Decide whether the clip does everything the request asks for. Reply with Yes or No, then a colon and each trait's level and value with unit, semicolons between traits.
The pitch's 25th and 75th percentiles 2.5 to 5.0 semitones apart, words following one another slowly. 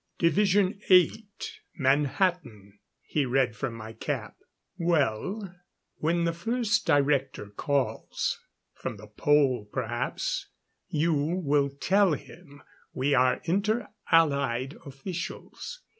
No: wide, 5.4 semitones; slow, 100 wpm